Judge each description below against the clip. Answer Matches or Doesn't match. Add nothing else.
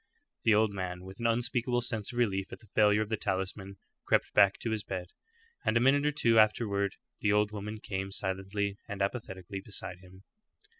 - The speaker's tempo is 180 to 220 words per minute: Matches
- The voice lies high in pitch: Doesn't match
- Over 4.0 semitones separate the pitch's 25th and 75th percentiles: Doesn't match